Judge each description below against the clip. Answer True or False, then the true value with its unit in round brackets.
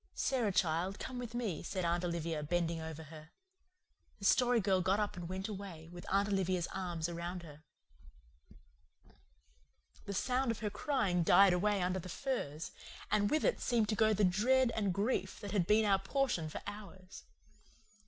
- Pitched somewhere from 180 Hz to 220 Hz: True (190 Hz)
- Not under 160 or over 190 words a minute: True (175 wpm)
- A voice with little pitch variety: False (3.7 semitones)